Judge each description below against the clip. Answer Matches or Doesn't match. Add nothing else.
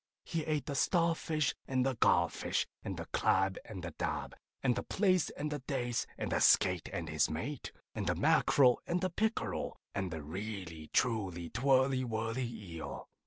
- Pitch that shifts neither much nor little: Doesn't match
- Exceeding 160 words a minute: Matches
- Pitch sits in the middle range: Doesn't match